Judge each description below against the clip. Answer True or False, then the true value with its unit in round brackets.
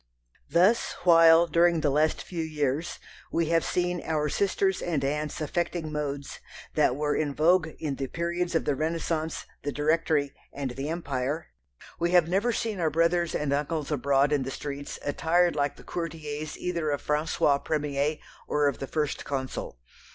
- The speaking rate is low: False (165 wpm)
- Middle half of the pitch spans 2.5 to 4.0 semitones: True (2.8 semitones)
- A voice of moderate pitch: True (155 Hz)